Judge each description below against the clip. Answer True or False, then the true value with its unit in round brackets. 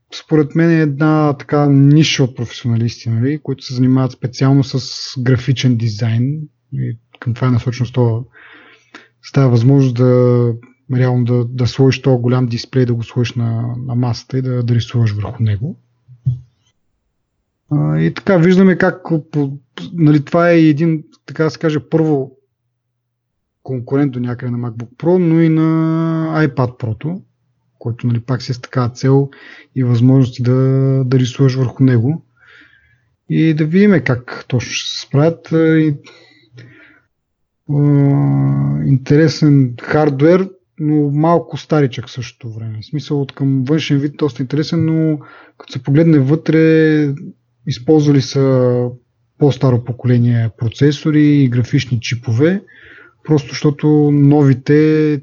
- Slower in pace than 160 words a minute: True (130 wpm)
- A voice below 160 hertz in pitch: True (135 Hz)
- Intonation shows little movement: False (3.7 semitones)